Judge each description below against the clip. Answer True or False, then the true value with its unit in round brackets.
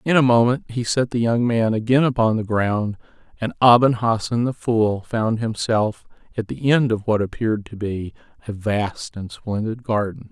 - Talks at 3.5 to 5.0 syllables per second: True (4.6 syllables/s)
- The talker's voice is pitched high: False (115 Hz)